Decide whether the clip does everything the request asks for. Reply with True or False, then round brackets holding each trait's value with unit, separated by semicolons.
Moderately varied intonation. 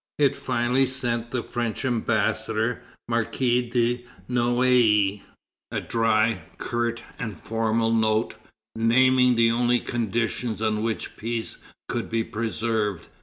False (1.6 semitones)